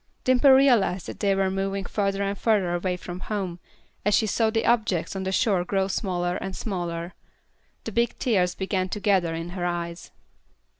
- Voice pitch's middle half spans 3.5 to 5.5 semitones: No, average, 2.8 semitones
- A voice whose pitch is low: No, high, 195 Hz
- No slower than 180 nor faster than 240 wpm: Yes, average, 185 wpm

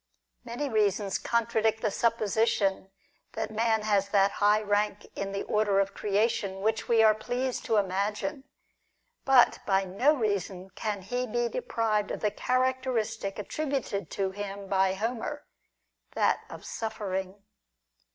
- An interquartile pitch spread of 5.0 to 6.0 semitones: No, average, 2.8 semitones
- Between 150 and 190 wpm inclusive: No, average, 140 wpm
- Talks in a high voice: Yes, high, 215 Hz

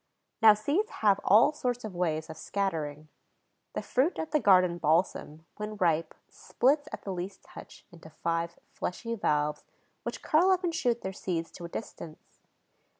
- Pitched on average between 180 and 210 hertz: Yes, high, 190 Hz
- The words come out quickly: No, average, 165 wpm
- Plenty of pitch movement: Yes, wide, 6.4 semitones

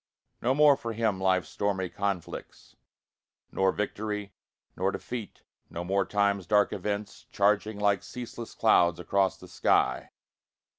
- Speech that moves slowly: Yes, slow, 130 wpm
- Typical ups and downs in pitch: No, narrow, 2.1 semitones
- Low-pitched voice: Yes, low, 100 Hz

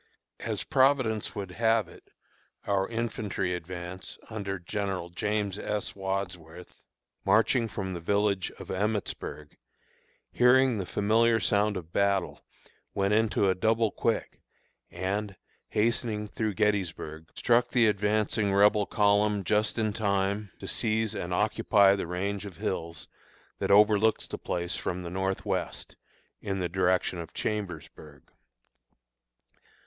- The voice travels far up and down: No, narrow, 2.5 semitones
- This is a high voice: No, low, 100 Hz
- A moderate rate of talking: No, slow, 125 wpm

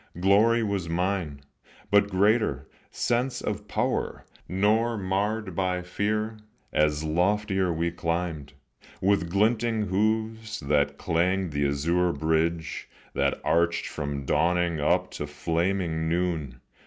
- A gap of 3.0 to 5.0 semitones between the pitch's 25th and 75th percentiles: Yes, average, 4.2 semitones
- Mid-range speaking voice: No, very low, 90 Hz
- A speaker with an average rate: No, slow, 115 wpm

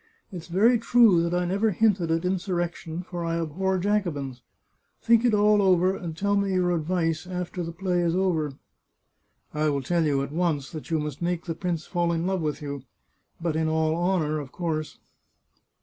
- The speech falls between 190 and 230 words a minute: Yes, average, 195 wpm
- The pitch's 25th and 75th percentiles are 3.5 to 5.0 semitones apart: No, average, 2.9 semitones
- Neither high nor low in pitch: Yes, medium, 175 Hz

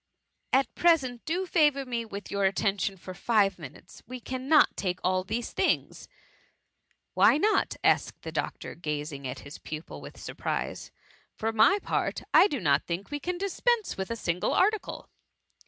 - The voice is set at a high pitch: Yes, high, 225 Hz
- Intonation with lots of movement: Yes, wide, 8.2 semitones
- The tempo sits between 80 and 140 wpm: No, average, 170 wpm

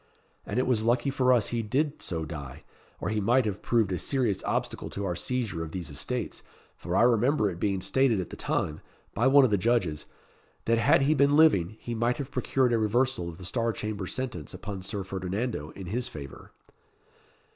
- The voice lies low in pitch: Yes, low, 110 Hz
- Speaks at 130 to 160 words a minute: No, fast, 205 wpm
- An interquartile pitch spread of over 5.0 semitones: Yes, wide, 5.4 semitones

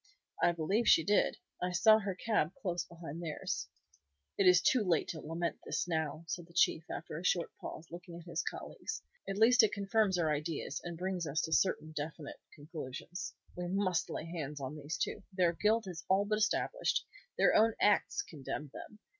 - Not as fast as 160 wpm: No, average, 190 wpm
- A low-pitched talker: No, medium, 175 Hz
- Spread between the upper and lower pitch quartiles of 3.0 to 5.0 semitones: Yes, average, 3.8 semitones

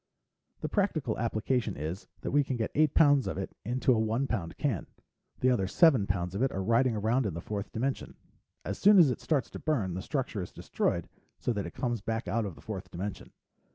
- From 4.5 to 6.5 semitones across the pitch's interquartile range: Yes, average, 5.2 semitones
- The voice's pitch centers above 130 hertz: No, low, 115 Hz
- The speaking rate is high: Yes, fast, 225 wpm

